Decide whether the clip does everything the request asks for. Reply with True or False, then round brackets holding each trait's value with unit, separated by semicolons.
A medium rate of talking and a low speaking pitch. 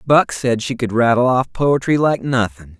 True (195 wpm; 120 Hz)